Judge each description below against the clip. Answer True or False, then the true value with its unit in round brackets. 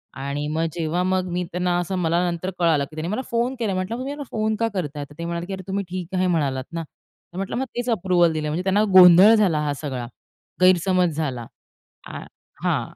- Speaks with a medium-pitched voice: True (180 Hz)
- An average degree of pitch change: True (3.2 semitones)